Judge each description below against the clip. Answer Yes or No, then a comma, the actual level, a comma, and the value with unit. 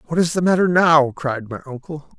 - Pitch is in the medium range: Yes, medium, 155 Hz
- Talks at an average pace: No, fast, 220 wpm